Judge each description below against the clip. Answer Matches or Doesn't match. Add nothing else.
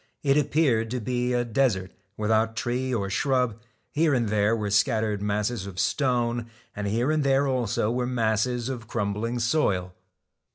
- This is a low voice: Matches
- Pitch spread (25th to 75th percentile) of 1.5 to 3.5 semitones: Matches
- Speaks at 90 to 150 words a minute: Doesn't match